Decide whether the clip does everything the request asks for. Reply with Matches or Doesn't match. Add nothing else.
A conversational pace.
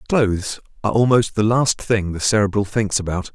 Matches